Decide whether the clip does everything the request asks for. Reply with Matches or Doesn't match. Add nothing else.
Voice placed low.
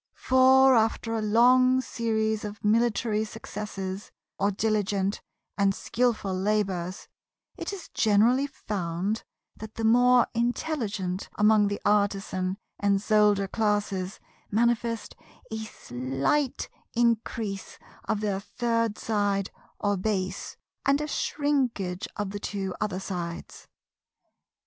Doesn't match